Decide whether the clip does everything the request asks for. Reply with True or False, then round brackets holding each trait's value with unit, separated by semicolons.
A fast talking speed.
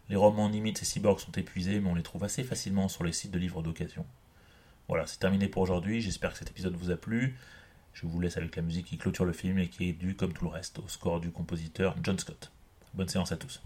True (260 wpm)